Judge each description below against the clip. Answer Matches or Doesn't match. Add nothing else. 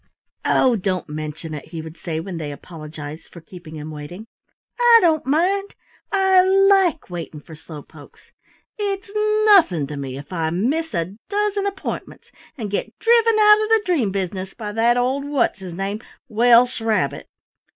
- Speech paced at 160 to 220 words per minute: Matches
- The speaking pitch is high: Matches